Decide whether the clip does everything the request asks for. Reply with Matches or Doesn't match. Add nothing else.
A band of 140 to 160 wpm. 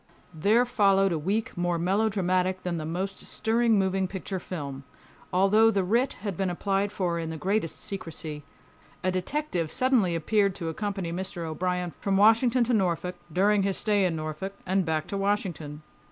Doesn't match